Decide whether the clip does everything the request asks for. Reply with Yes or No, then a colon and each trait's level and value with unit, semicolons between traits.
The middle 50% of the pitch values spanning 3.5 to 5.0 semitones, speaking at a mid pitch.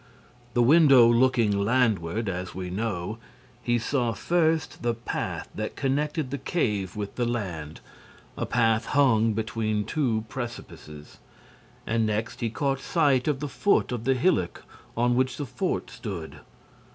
No: average, 3.8 semitones; low, 120 Hz